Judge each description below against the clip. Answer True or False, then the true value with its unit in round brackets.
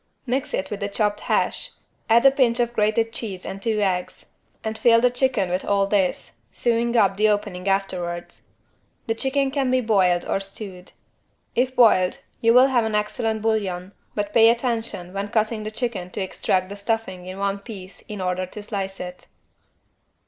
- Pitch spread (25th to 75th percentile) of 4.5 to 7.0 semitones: False (3.4 semitones)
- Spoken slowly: False (180 wpm)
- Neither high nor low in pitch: False (210 Hz)